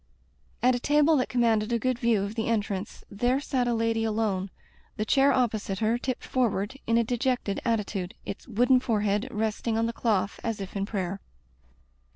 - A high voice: Yes, high, 225 Hz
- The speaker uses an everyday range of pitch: Yes, average, 3.1 semitones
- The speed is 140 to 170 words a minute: No, average, 190 wpm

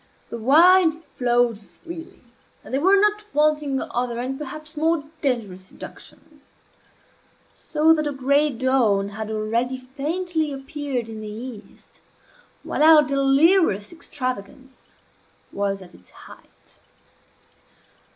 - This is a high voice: Yes, very high, 270 Hz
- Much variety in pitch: No, average, 4.8 semitones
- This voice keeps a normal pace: No, slow, 115 wpm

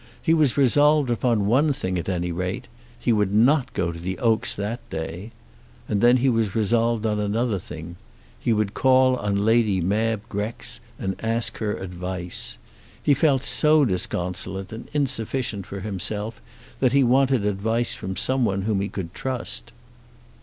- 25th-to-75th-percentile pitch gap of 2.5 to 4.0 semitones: No, average, 4.5 semitones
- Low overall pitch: Yes, low, 110 Hz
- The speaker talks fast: No, average, 160 wpm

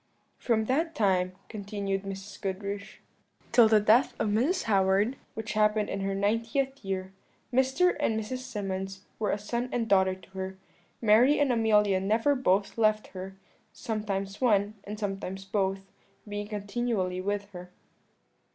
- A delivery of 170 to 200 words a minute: No, average, 145 wpm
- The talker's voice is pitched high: Yes, high, 205 Hz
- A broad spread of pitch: No, average, 2.8 semitones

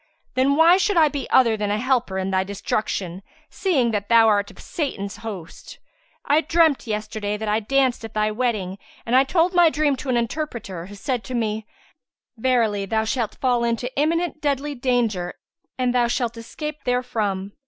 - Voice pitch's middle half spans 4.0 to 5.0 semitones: Yes, average, 4.5 semitones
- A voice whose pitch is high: Yes, high, 235 Hz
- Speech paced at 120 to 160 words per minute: No, average, 180 wpm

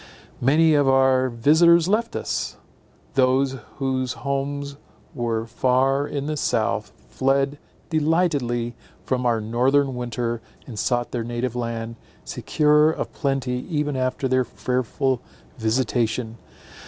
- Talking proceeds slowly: Yes, slow, 115 wpm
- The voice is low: Yes, low, 130 Hz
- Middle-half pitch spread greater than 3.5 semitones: No, average, 2.9 semitones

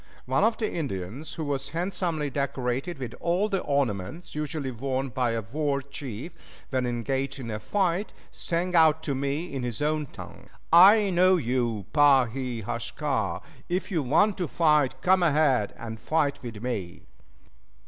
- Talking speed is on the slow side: No, average, 160 wpm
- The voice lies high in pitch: No, medium, 140 Hz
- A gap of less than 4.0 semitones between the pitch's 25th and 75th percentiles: No, average, 5.2 semitones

